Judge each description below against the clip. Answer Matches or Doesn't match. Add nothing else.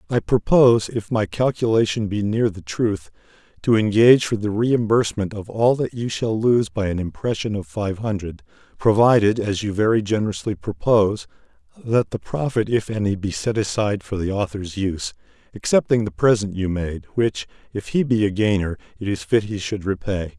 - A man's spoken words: Matches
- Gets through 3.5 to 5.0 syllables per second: Doesn't match